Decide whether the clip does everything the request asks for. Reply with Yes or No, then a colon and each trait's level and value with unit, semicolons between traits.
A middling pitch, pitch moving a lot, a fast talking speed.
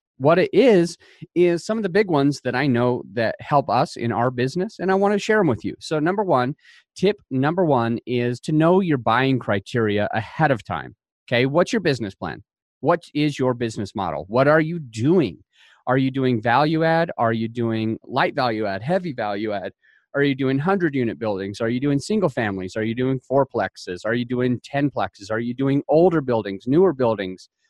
No: low, 130 Hz; wide, 5.9 semitones; fast, 210 wpm